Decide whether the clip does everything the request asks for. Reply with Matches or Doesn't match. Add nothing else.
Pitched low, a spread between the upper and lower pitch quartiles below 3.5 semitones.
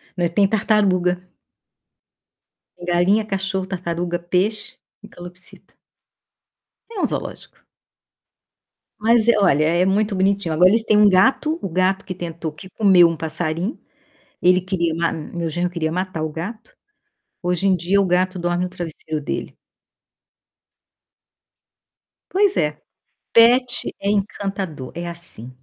Doesn't match